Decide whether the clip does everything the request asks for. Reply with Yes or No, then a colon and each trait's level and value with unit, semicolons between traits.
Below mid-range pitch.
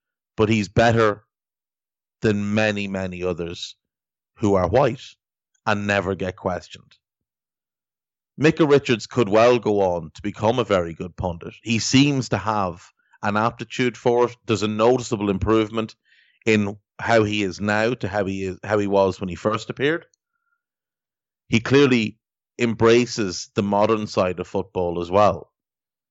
Yes: low, 110 Hz